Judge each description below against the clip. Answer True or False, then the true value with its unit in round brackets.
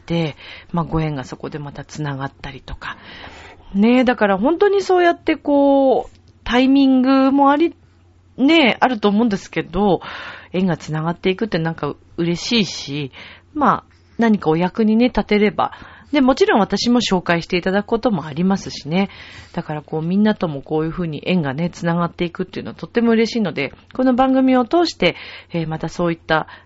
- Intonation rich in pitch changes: True (7.5 semitones)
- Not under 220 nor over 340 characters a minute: False (375 characters per minute)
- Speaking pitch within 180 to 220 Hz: True (185 Hz)